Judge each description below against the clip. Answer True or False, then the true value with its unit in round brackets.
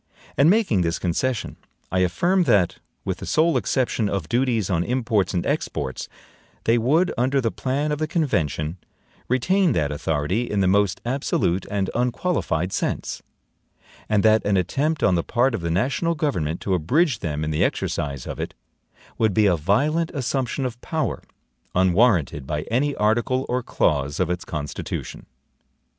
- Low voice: True (110 Hz)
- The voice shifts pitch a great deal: True (7.3 semitones)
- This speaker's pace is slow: False (160 wpm)